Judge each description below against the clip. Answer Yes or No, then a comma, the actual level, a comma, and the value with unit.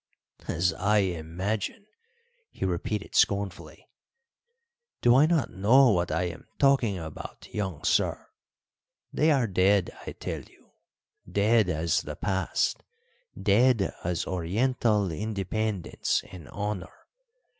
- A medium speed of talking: No, slow, 115 wpm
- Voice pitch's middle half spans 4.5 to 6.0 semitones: No, average, 3.8 semitones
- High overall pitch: No, low, 100 Hz